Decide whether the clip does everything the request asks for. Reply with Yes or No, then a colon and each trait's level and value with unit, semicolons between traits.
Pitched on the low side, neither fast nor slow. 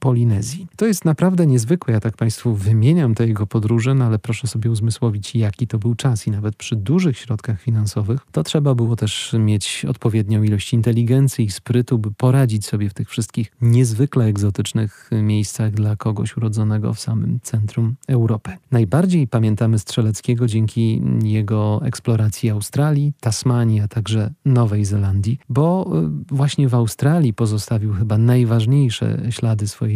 Yes: low, 115 Hz; average, 150 wpm